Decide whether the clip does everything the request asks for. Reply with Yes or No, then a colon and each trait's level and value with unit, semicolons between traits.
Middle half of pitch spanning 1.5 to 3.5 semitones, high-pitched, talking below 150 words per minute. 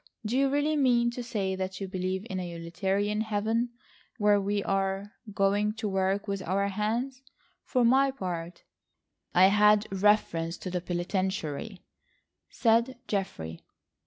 Yes: average, 3.0 semitones; high, 200 Hz; average, 140 wpm